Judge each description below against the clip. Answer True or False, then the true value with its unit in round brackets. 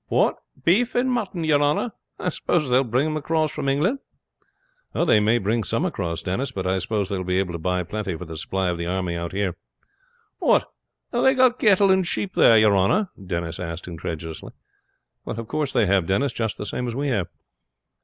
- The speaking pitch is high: False (110 Hz)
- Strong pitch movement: True (9.0 semitones)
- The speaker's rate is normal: False (210 wpm)